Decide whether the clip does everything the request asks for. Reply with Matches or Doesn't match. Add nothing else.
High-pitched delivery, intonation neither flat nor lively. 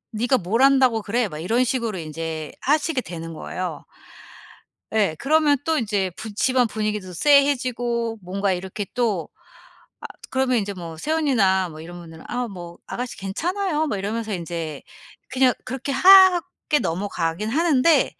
Doesn't match